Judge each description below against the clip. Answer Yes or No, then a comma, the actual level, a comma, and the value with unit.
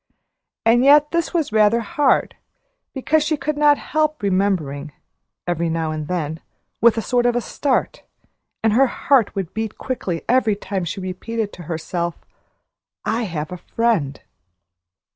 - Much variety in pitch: Yes, wide, 7.0 semitones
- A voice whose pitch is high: Yes, high, 215 Hz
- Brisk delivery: No, average, 145 wpm